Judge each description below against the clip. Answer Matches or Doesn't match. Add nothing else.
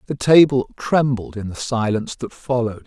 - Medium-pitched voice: Doesn't match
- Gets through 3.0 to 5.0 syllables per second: Doesn't match